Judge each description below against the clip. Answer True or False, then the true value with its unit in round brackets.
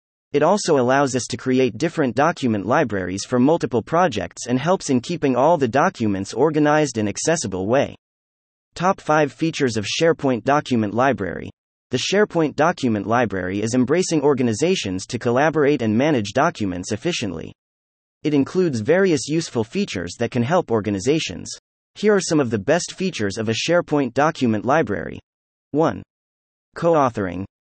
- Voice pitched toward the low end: True (130 Hz)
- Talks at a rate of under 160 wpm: True (145 wpm)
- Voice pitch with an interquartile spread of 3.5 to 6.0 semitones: False (6.7 semitones)